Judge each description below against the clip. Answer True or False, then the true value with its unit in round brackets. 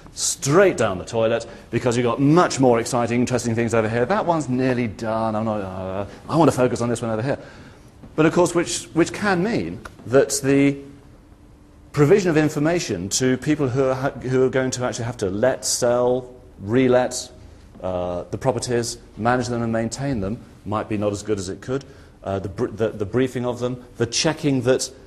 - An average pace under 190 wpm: False (200 wpm)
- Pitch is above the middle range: False (125 Hz)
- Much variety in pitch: False (3.7 semitones)